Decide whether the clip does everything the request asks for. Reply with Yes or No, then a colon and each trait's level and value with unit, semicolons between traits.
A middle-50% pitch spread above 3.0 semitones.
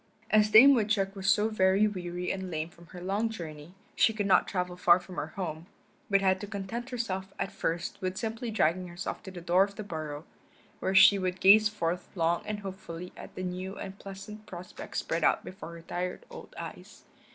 No: average, 2.7 semitones